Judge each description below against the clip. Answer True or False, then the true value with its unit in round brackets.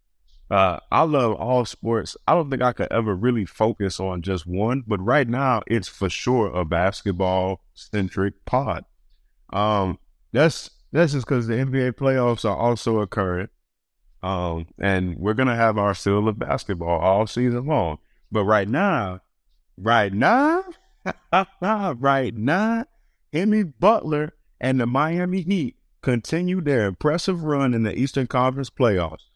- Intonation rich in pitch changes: True (6.2 semitones)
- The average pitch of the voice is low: True (115 Hz)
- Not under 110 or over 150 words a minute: True (145 wpm)